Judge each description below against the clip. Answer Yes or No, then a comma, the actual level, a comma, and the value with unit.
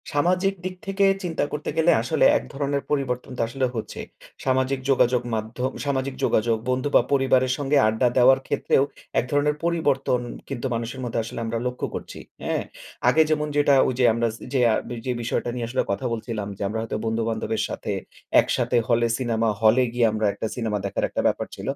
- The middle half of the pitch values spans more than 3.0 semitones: Yes, average, 3.5 semitones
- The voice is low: Yes, low, 130 Hz